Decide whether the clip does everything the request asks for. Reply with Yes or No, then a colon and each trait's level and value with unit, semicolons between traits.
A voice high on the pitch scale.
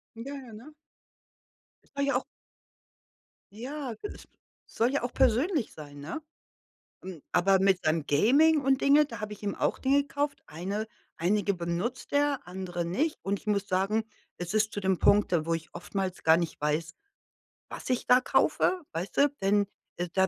Yes: high, 210 Hz